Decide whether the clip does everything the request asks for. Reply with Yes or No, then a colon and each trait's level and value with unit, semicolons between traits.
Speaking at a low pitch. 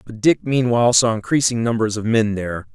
Yes: low, 115 Hz